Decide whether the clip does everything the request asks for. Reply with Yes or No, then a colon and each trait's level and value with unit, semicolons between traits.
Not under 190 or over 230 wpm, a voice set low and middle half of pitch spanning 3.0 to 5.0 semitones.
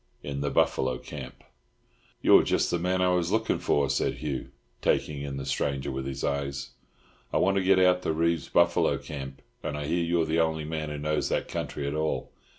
Yes: fast, 205 wpm; very low, 75 Hz; average, 3.6 semitones